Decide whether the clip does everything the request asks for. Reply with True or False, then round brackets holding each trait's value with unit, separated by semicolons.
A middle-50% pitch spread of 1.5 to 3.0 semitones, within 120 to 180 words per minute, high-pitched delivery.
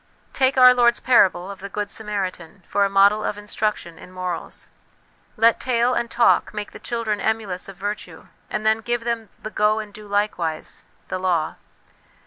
False (2.7 semitones; 190 wpm; 210 Hz)